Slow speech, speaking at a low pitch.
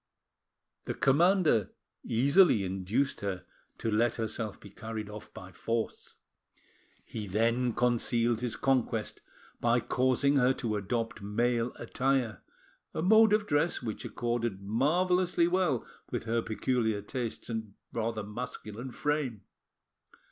Yes: slow, 120 wpm; low, 120 Hz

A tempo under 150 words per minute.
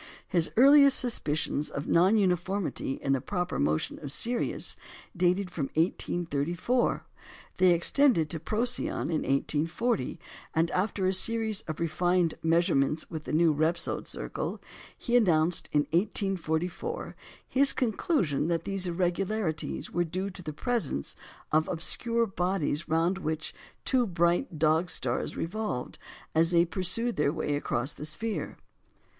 Yes: slow, 135 wpm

